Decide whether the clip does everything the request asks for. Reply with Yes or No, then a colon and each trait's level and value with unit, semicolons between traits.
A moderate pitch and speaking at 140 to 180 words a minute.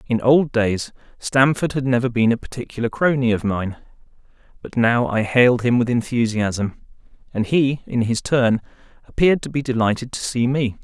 No: low, 120 Hz; average, 170 wpm